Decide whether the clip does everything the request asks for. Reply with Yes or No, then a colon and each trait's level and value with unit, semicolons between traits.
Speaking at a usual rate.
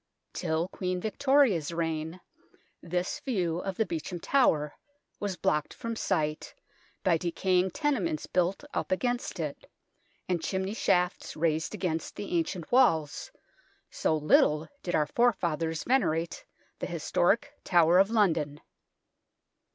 No: slow, 120 wpm